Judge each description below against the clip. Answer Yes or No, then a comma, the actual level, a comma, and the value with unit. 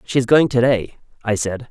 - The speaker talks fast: Yes, fast, 210 wpm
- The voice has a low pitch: Yes, low, 120 Hz